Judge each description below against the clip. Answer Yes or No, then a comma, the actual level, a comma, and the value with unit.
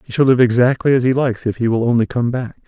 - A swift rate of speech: Yes, fast, 290 wpm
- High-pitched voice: No, low, 120 Hz